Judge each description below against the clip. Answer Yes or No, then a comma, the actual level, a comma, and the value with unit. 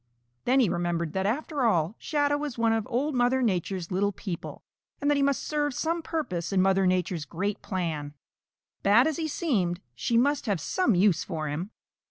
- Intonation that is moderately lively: No, wide, 7.9 semitones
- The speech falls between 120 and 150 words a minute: No, average, 190 wpm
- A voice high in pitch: Yes, high, 205 Hz